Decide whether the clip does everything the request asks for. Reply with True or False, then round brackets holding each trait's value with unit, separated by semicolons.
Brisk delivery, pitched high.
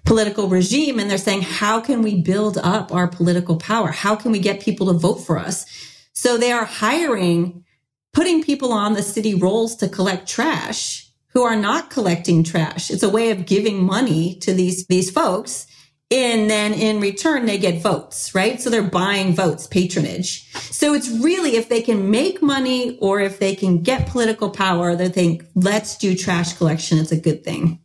False (190 wpm; 195 Hz)